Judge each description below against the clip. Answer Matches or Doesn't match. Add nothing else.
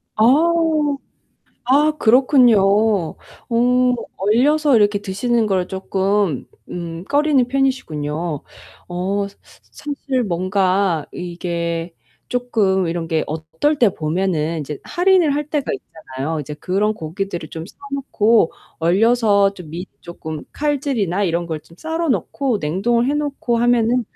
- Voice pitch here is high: Matches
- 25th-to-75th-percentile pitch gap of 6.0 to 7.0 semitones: Matches